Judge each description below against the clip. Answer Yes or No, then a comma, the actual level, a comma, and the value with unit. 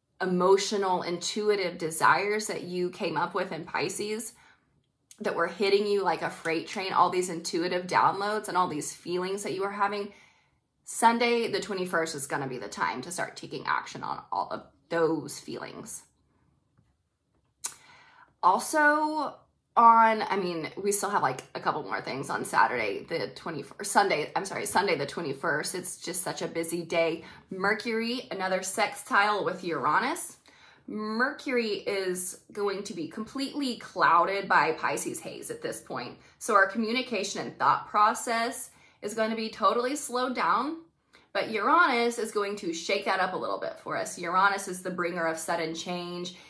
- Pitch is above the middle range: Yes, high, 200 Hz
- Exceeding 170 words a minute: No, average, 165 wpm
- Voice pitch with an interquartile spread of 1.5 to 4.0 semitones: No, average, 4.4 semitones